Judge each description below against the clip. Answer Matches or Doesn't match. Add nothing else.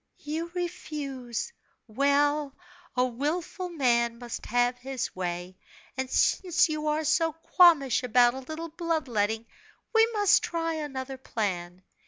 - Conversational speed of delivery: Doesn't match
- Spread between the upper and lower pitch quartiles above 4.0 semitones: Matches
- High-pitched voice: Matches